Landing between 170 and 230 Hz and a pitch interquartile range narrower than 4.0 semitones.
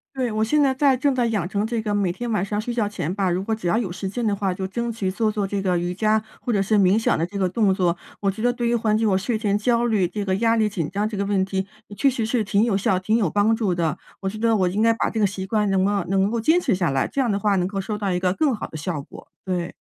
Yes: high, 205 Hz; average, 3.0 semitones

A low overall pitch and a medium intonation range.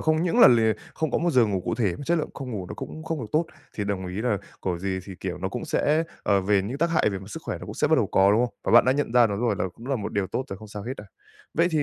No: low, 115 Hz; wide, 6.9 semitones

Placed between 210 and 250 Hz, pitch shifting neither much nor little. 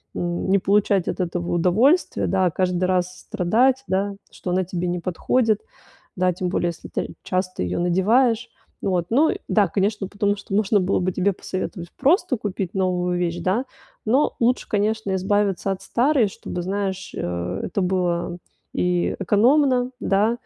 No: high, 190 Hz; average, 3.2 semitones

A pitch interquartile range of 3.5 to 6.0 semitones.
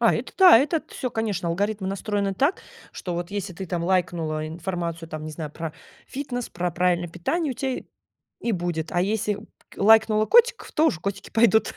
Yes: average, 4.6 semitones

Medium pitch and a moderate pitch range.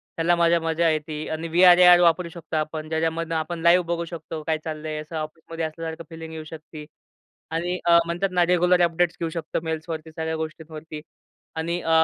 No: medium, 165 Hz; narrow, 1.3 semitones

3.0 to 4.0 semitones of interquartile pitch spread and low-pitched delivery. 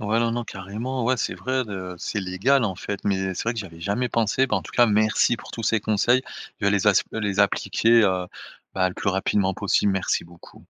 Yes: average, 3.3 semitones; low, 105 Hz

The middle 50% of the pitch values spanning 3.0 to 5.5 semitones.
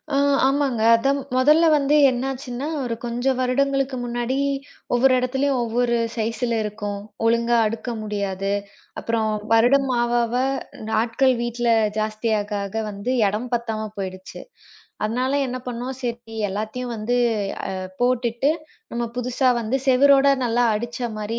No: narrow, 2.6 semitones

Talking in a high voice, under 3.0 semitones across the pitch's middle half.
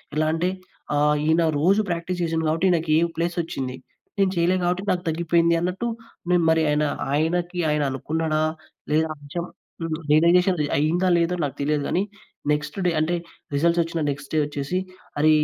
No: medium, 165 Hz; narrow, 2.5 semitones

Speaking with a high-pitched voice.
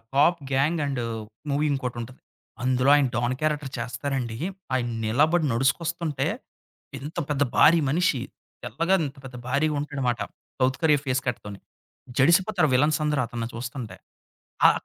No: low, 135 Hz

